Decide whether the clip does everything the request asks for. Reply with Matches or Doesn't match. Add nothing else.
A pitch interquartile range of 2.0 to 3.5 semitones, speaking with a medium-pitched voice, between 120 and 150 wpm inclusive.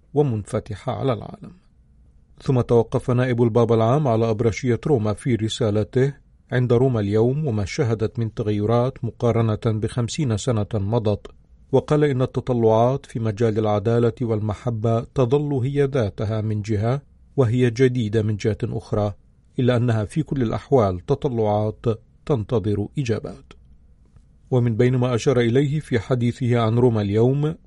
Doesn't match